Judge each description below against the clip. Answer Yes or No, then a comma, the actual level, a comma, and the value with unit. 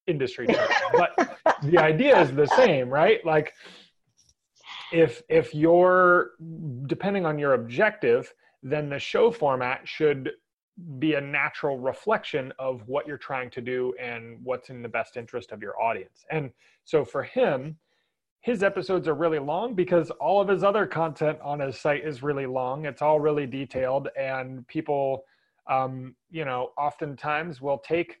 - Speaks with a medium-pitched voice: Yes, medium, 150 Hz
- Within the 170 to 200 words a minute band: No, average, 155 wpm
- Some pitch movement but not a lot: Yes, average, 4.1 semitones